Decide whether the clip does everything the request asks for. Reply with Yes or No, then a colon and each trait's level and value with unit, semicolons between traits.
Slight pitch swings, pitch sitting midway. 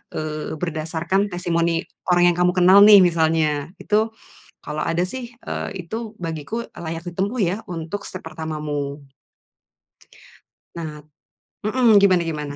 No: average, 3.6 semitones; medium, 170 Hz